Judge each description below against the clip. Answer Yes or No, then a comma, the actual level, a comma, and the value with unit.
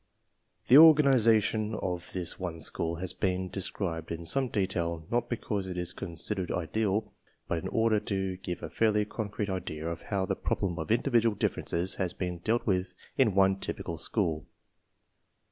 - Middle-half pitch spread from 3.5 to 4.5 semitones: Yes, average, 3.8 semitones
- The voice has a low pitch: Yes, very low, 95 Hz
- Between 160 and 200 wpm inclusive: Yes, average, 170 wpm